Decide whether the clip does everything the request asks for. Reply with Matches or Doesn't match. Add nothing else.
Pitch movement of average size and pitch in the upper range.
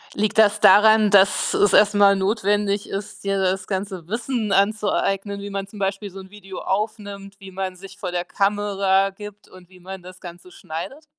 Doesn't match